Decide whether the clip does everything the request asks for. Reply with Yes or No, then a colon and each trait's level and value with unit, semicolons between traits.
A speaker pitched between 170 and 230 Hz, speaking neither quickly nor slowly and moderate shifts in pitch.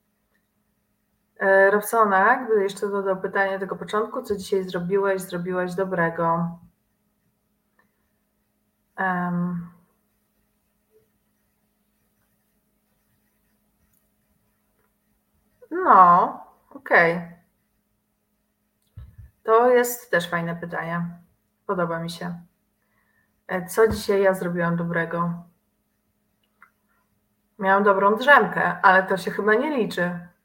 No: high, 190 Hz; slow, 80 wpm; average, 3.1 semitones